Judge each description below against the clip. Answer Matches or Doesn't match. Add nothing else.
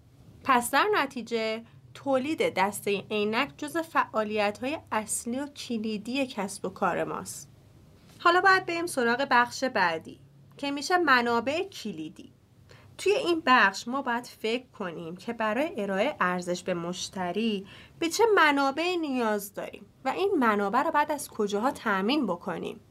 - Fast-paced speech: Doesn't match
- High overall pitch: Matches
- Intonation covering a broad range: Matches